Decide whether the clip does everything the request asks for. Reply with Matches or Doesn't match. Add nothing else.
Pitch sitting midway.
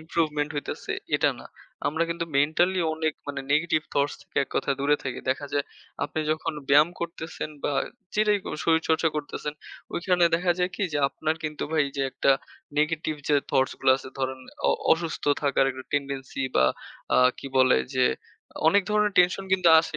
Matches